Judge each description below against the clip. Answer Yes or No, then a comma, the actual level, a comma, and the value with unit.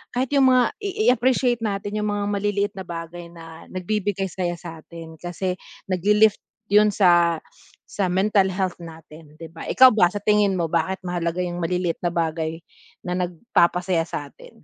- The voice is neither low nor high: Yes, medium, 180 Hz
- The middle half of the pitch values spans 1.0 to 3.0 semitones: No, average, 3.6 semitones